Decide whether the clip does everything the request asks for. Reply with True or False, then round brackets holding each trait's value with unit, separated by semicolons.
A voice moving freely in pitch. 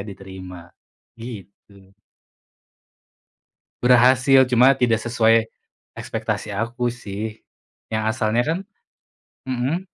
False (3.7 semitones)